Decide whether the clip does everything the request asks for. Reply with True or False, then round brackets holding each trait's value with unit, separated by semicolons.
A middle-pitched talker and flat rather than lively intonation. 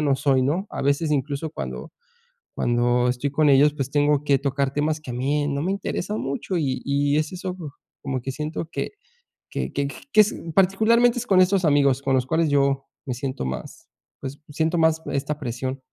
False (145 Hz; 3.0 semitones)